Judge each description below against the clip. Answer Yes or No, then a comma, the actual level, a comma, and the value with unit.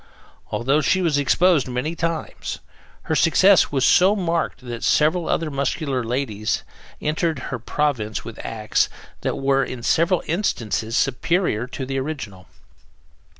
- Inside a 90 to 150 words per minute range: Yes, slow, 135 wpm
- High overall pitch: No, medium, 140 Hz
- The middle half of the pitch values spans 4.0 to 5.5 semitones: Yes, average, 5.1 semitones